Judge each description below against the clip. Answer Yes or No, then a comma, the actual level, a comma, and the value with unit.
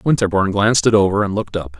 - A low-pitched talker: Yes, low, 100 Hz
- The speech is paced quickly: Yes, fast, 235 wpm